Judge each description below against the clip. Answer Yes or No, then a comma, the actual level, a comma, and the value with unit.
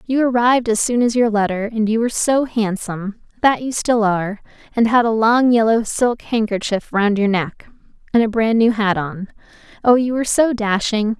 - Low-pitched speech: No, high, 225 Hz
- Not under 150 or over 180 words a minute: No, average, 190 wpm